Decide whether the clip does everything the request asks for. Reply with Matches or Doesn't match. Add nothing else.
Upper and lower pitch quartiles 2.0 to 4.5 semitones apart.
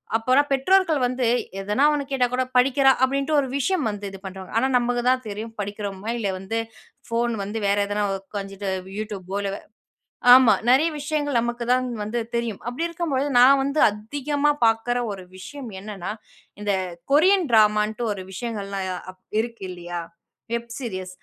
Doesn't match